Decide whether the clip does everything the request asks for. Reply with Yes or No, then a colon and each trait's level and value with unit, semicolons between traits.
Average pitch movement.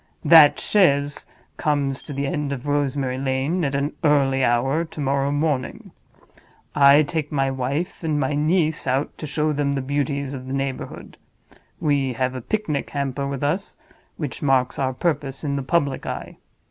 No: narrow, 1.8 semitones